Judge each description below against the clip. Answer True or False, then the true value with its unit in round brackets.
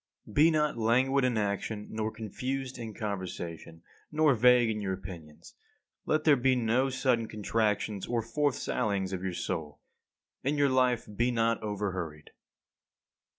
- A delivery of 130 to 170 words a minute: True (150 wpm)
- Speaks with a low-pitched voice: True (115 Hz)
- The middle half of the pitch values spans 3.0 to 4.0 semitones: False (4.4 semitones)